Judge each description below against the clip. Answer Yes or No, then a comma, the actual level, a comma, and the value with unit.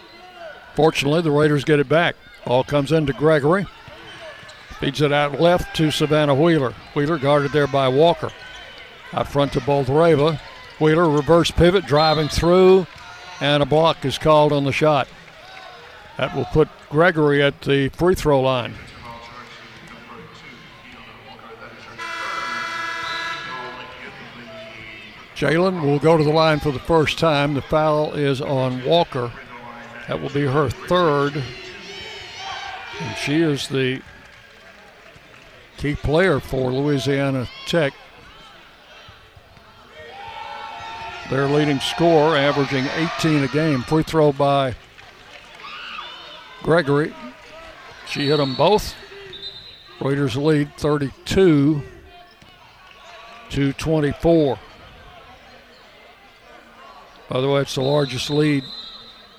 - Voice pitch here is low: No, medium, 145 Hz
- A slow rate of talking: Yes, slow, 105 wpm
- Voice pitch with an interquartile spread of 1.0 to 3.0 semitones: Yes, narrow, 2.6 semitones